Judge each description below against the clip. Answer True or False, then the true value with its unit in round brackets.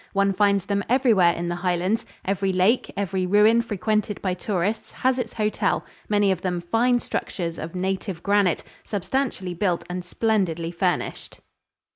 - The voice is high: True (195 Hz)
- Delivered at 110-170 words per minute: True (150 wpm)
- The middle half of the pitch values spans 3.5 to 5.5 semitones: False (3.0 semitones)